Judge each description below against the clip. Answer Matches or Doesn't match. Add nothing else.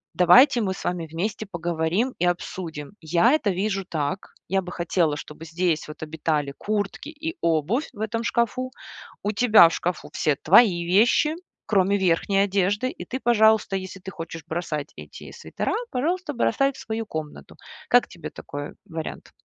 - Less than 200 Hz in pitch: Matches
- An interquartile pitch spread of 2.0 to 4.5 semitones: Doesn't match